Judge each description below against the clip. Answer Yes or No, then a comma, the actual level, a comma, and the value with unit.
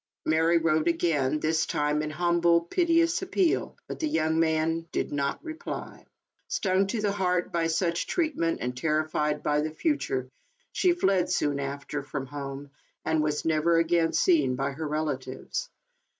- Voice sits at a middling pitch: Yes, medium, 160 Hz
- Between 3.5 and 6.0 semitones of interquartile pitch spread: No, average, 3.1 semitones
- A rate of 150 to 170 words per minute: Yes, average, 155 wpm